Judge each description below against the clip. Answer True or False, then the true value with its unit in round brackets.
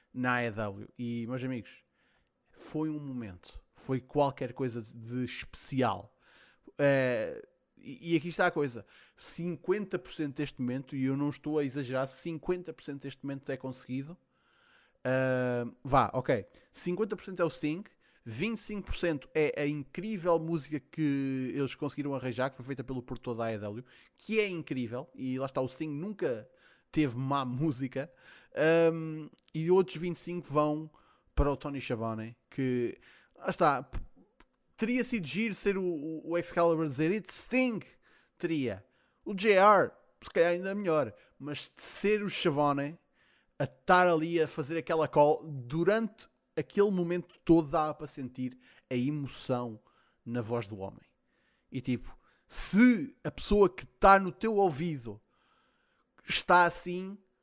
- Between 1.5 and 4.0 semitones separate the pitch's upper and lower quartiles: False (5.2 semitones)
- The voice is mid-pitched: True (150 Hz)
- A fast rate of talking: False (145 wpm)